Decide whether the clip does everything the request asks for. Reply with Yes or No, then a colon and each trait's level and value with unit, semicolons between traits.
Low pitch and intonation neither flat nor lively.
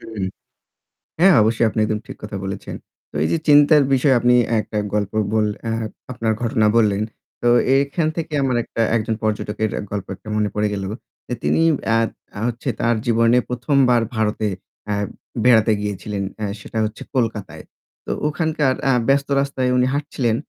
Yes: low, 115 Hz; average, 3.7 semitones